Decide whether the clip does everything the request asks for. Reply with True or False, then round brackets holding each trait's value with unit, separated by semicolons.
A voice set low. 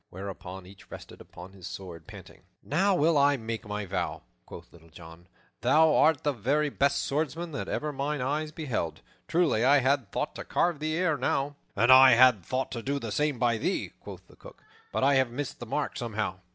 True (130 Hz)